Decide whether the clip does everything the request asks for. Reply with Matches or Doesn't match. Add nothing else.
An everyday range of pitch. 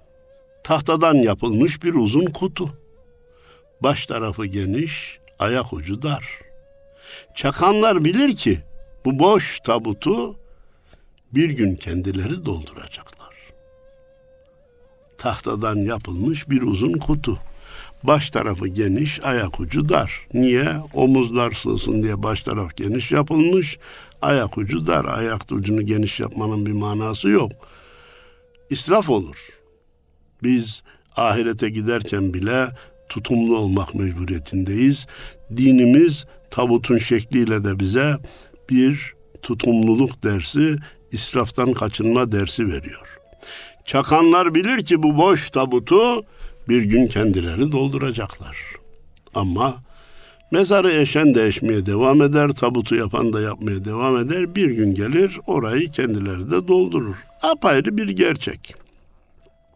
Doesn't match